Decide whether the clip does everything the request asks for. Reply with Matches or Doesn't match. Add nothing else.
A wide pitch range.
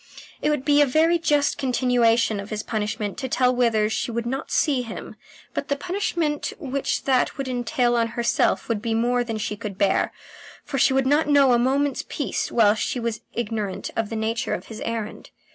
Doesn't match